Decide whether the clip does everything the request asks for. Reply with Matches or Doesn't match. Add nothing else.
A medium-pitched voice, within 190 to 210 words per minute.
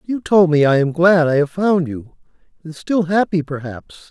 Matches